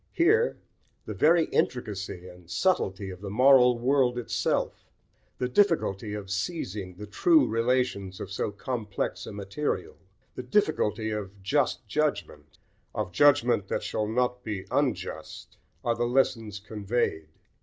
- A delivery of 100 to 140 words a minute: Yes, slow, 135 wpm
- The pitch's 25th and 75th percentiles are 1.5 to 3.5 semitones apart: No, average, 4.8 semitones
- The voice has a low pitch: Yes, low, 115 Hz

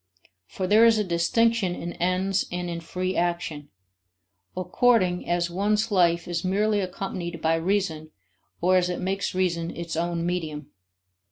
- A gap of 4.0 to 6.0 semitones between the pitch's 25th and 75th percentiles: No, narrow, 2.4 semitones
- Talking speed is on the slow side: No, average, 150 wpm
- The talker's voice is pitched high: No, medium, 180 Hz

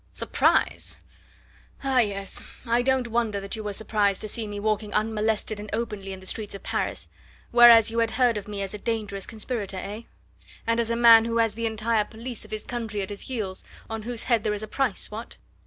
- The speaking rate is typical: No, fast, 215 wpm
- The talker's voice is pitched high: Yes, high, 220 Hz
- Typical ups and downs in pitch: No, narrow, 2.0 semitones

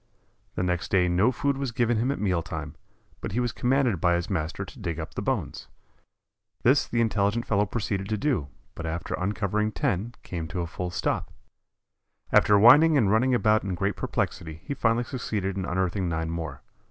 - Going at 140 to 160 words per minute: No, average, 190 wpm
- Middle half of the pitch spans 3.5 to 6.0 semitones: Yes, average, 5.0 semitones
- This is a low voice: Yes, low, 100 Hz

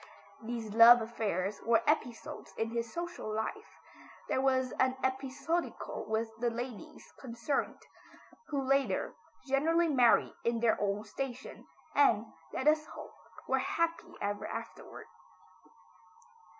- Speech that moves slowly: Yes, slow, 120 wpm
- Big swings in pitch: No, average, 3.9 semitones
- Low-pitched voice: No, high, 245 Hz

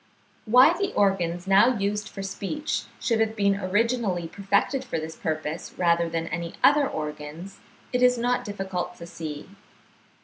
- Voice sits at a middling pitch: No, high, 195 Hz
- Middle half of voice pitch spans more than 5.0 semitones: Yes, wide, 5.4 semitones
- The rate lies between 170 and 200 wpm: No, average, 150 wpm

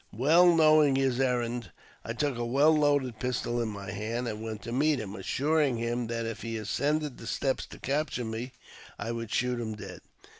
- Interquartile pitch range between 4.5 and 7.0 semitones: No, average, 3.8 semitones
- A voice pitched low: Yes, low, 120 Hz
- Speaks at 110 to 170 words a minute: No, average, 195 wpm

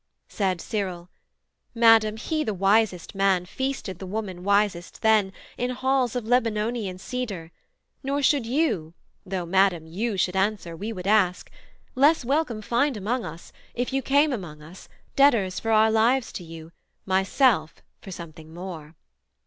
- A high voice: Yes, high, 210 Hz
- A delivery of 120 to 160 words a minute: Yes, average, 150 wpm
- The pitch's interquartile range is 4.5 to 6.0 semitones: Yes, average, 5.0 semitones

